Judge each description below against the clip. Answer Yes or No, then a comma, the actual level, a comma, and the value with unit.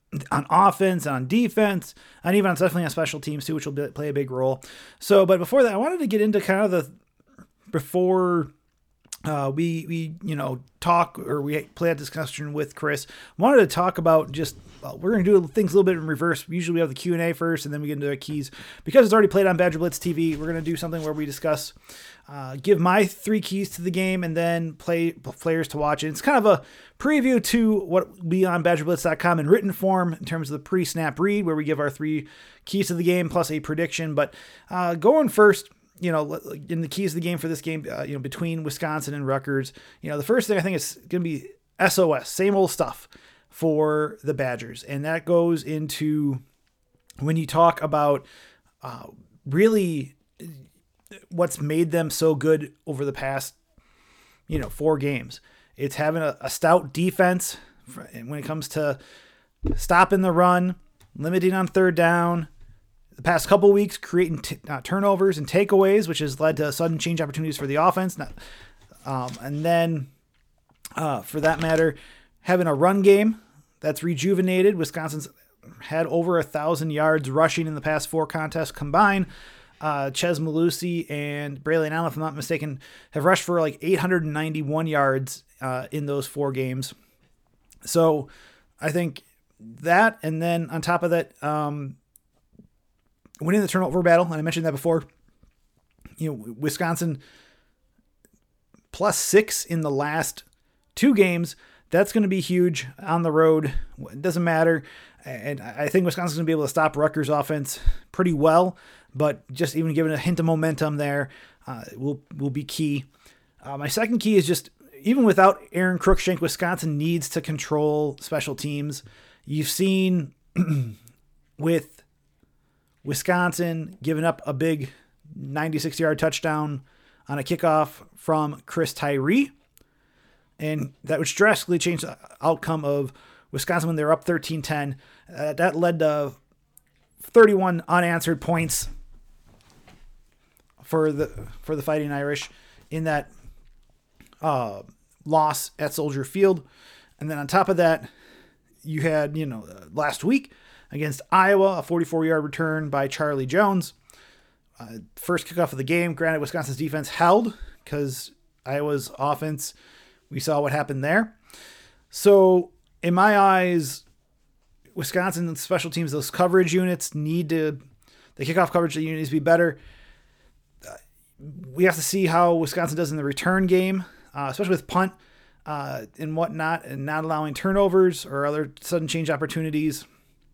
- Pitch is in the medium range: Yes, medium, 160 Hz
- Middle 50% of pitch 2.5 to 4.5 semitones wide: Yes, average, 3.2 semitones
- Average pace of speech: Yes, average, 170 wpm